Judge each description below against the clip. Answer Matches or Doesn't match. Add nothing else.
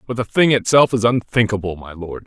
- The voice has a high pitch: Doesn't match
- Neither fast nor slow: Doesn't match